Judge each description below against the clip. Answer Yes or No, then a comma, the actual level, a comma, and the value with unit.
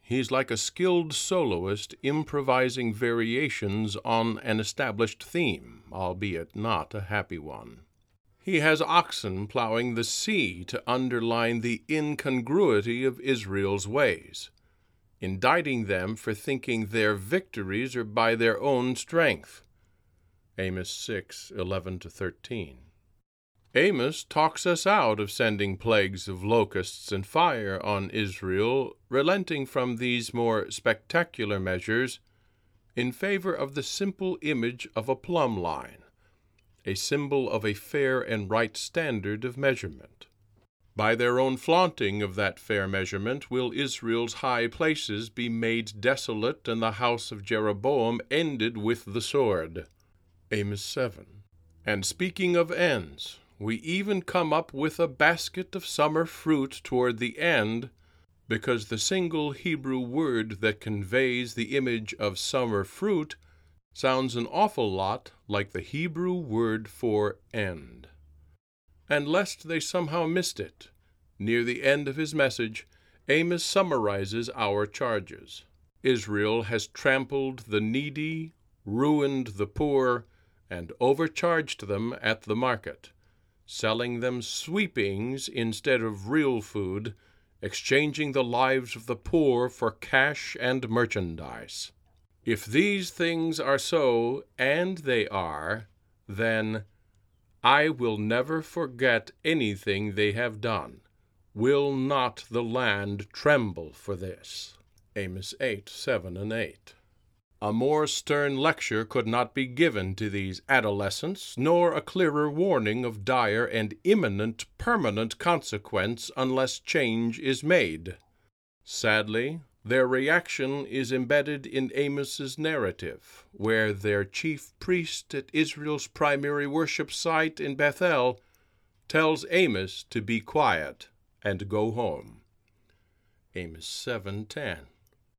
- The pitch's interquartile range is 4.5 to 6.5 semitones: Yes, average, 5.3 semitones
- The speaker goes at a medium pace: No, slow, 125 wpm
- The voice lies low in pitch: Yes, low, 115 Hz